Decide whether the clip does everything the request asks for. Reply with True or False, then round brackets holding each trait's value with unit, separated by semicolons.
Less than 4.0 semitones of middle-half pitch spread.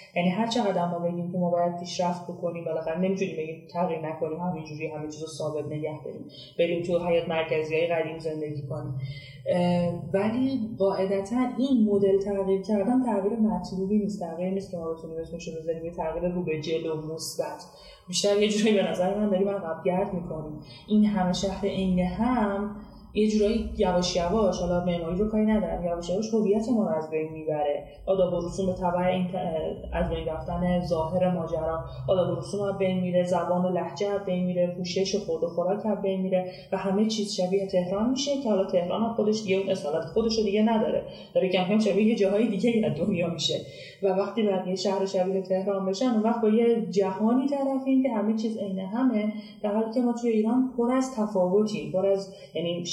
True (3.3 semitones)